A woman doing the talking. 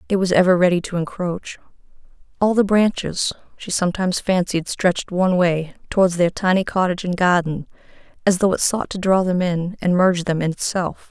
Yes: female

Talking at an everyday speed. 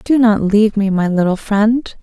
No: fast, 210 wpm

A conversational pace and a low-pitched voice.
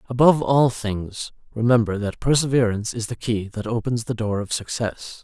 Yes: average, 170 wpm; low, 115 Hz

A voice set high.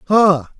No: medium, 180 Hz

